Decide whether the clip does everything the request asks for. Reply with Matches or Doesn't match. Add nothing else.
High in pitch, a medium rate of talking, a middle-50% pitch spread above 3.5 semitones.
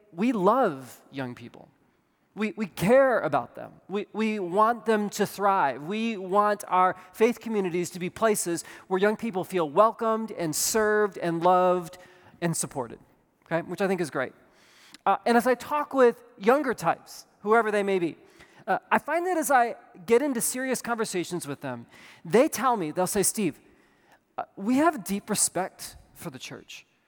Matches